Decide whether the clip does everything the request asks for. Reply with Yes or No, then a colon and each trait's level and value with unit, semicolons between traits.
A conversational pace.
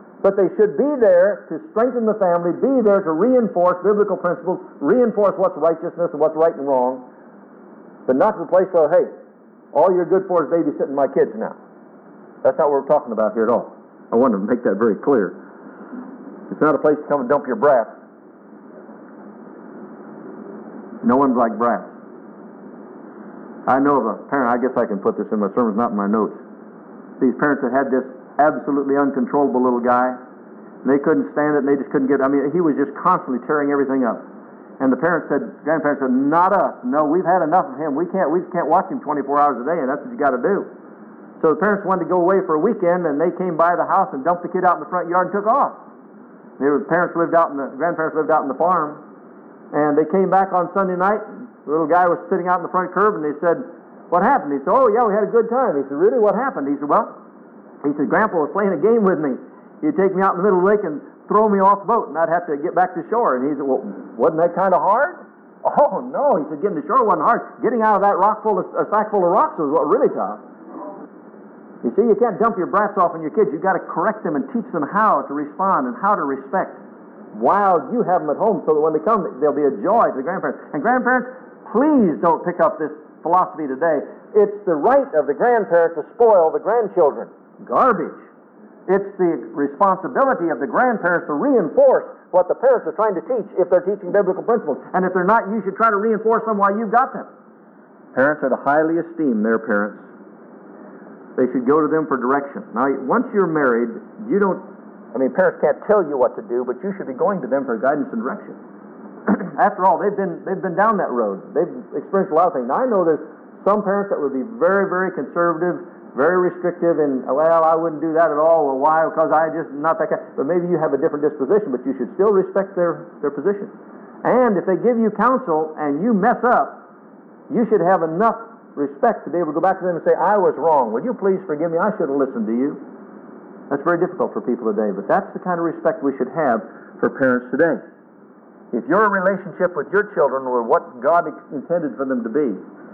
No: fast, 235 wpm